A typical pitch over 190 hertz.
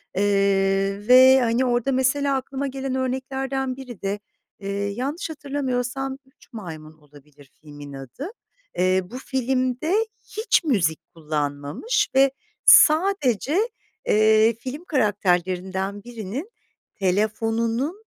Yes: high, 235 Hz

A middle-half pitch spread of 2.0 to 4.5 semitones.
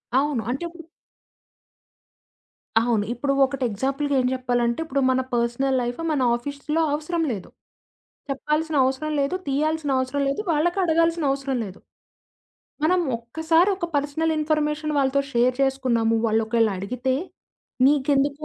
Yes: average, 3.7 semitones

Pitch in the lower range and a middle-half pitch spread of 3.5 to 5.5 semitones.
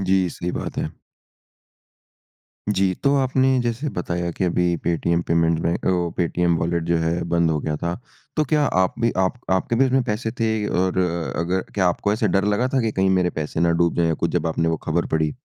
Yes: very low, 90 Hz; average, 3.9 semitones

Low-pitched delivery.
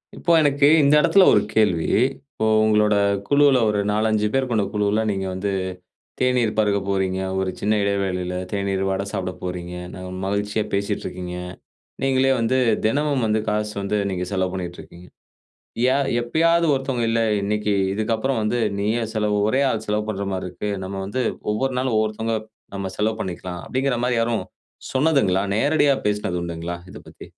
Yes: low, 105 Hz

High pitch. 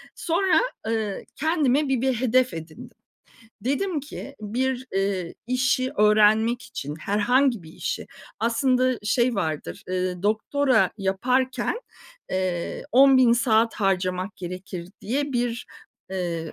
Yes: high, 230 Hz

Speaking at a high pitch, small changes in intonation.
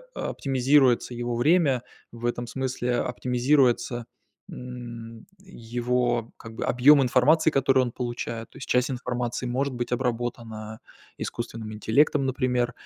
No: low, 125 Hz; narrow, 1.8 semitones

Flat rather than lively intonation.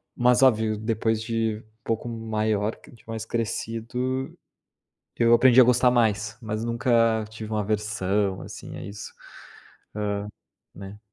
Yes: narrow, 1.6 semitones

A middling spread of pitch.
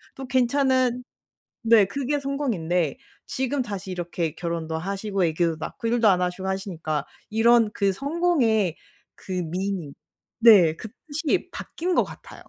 No: wide, 6.5 semitones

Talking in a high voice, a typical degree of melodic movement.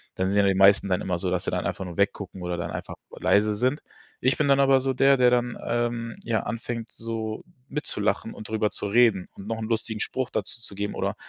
No: low, 110 Hz; average, 3.4 semitones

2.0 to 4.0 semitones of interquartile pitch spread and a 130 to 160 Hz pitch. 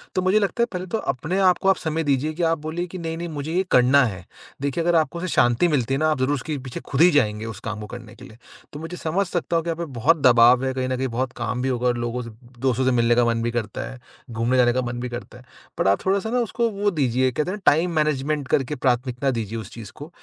No: average, 5.3 semitones; low, 135 Hz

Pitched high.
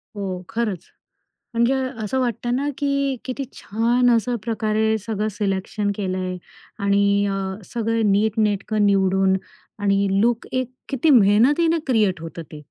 Yes: high, 215 Hz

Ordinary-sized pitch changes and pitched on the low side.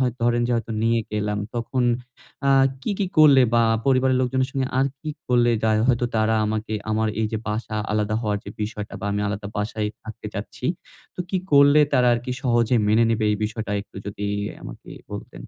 Yes: average, 3.0 semitones; low, 115 Hz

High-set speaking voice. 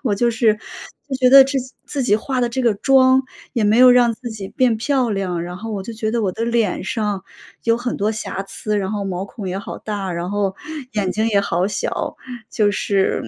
Yes: high, 215 Hz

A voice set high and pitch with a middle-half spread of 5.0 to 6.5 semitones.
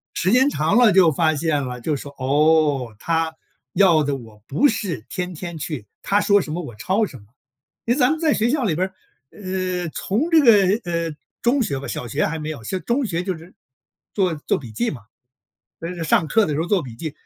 No: medium, 170 Hz; wide, 5.4 semitones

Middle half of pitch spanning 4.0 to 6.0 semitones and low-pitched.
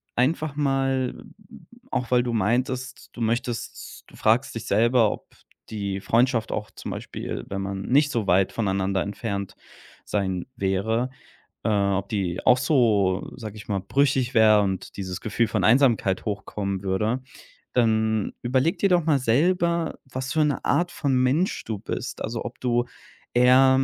Yes: average, 4.5 semitones; low, 115 Hz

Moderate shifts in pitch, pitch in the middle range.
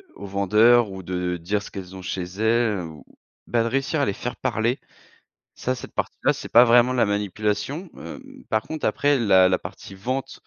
No: average, 4.2 semitones; low, 105 Hz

